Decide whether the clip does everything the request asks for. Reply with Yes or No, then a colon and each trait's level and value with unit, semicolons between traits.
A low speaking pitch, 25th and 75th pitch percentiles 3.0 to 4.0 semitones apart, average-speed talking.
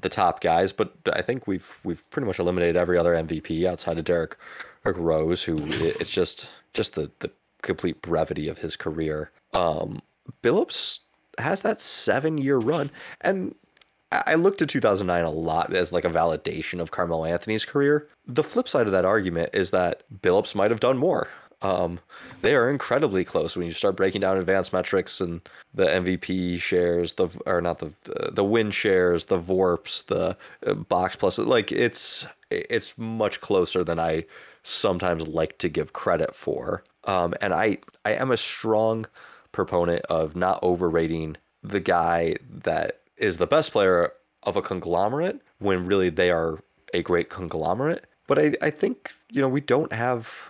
No: very low, 90 Hz; average, 4.6 semitones; average, 170 wpm